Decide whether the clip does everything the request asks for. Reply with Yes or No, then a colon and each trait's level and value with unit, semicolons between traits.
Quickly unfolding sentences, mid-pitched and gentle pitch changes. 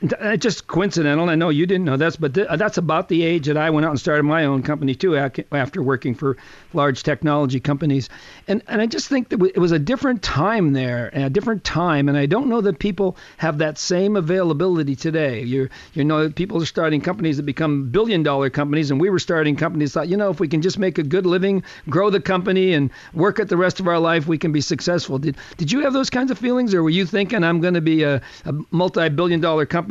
No: fast, 240 wpm; medium, 165 Hz; average, 4.0 semitones